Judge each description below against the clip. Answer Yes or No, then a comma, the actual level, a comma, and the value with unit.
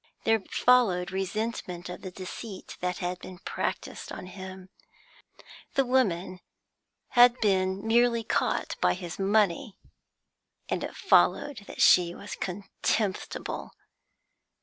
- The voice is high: Yes, high, 195 Hz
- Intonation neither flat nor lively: Yes, average, 3.6 semitones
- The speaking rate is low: Yes, slow, 115 wpm